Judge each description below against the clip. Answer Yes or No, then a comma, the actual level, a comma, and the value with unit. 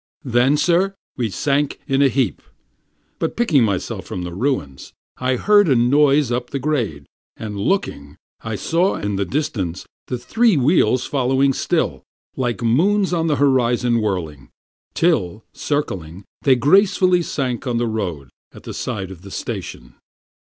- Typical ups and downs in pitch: No, wide, 6.5 semitones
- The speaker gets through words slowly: No, average, 150 wpm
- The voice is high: No, low, 125 Hz